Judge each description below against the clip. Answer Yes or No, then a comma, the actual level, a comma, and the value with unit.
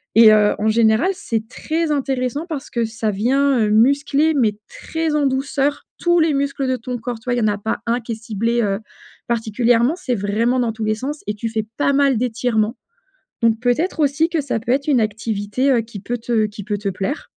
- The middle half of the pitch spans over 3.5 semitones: Yes, average, 4.2 semitones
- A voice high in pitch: Yes, high, 240 Hz